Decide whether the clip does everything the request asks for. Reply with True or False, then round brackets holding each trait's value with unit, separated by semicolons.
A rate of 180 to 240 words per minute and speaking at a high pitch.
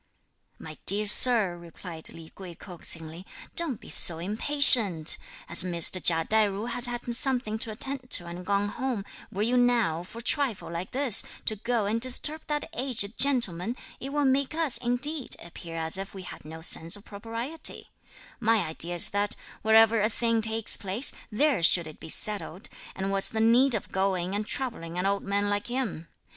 True (185 wpm; 210 Hz)